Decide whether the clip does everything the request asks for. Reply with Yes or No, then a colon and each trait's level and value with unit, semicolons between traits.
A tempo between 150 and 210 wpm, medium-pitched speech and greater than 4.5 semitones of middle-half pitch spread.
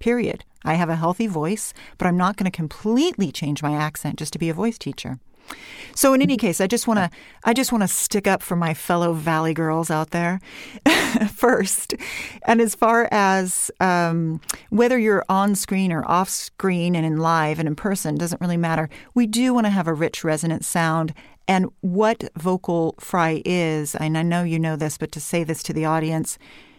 Yes: fast, 205 wpm; medium, 175 Hz; average, 4.9 semitones